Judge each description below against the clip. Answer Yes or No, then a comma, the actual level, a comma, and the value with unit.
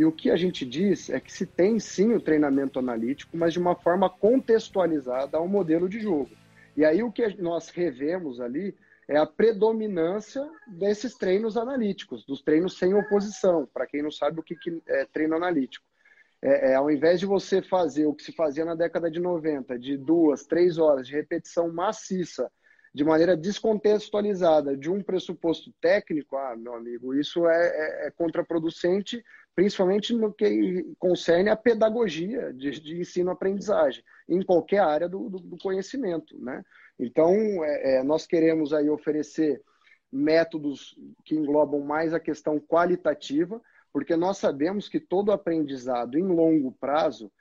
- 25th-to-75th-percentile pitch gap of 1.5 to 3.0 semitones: No, average, 4.6 semitones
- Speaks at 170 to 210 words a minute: No, average, 160 wpm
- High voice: No, medium, 170 Hz